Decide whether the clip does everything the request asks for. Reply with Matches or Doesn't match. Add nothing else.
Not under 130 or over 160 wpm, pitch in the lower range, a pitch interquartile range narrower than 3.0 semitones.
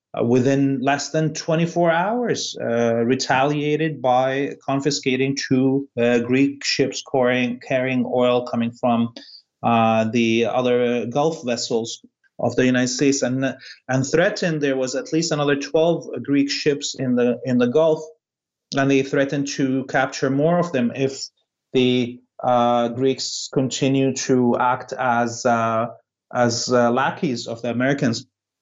Matches